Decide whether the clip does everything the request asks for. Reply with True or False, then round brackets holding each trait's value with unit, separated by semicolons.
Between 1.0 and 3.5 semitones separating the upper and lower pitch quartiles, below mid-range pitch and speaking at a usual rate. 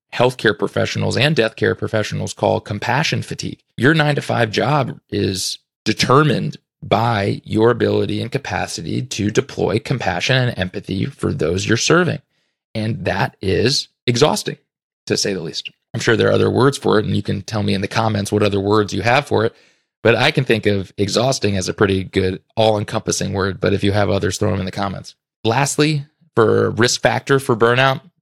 False (4.2 semitones; 110 Hz; 190 wpm)